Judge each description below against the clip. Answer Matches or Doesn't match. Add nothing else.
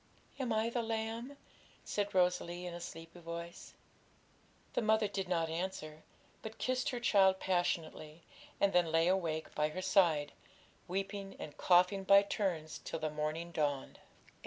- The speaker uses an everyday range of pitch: Matches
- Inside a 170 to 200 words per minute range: Doesn't match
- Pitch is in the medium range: Matches